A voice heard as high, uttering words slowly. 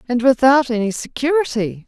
Yes: high, 240 Hz; slow, 130 wpm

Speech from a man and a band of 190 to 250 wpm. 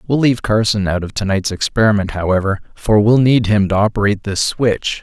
Yes: male; fast, 205 wpm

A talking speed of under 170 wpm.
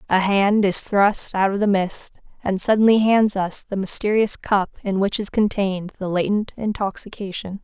No: average, 175 wpm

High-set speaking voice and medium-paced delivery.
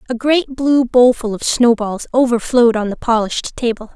Yes: high, 240 Hz; average, 165 wpm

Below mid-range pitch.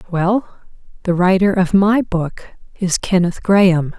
No: medium, 185 Hz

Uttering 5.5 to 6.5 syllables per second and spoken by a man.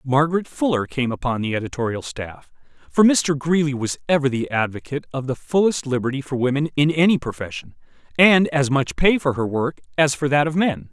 Yes: 5.6 syllables/s; male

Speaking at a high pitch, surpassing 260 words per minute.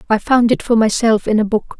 Yes: high, 225 Hz; fast, 270 wpm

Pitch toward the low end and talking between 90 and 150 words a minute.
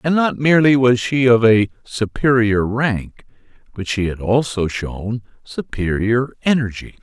Yes: low, 115 Hz; slow, 135 wpm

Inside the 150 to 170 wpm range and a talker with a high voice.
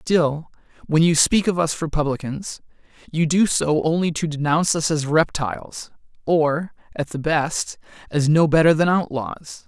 No: average, 155 wpm; medium, 160 Hz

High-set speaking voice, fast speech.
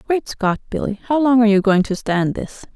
Yes: high, 220 Hz; fast, 240 wpm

